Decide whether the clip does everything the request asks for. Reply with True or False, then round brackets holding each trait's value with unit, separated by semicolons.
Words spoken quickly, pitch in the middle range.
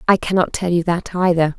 True (225 wpm; 175 Hz)